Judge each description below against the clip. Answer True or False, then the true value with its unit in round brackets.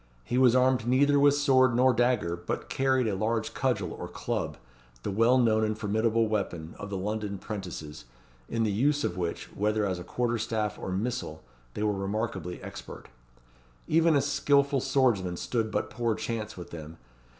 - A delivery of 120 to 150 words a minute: False (170 wpm)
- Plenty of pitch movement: False (4.4 semitones)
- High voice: False (110 Hz)